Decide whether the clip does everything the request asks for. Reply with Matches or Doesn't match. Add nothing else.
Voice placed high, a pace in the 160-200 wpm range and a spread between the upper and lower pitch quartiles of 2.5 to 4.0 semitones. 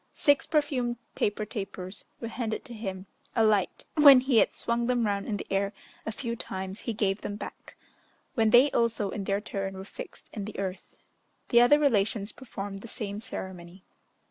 Matches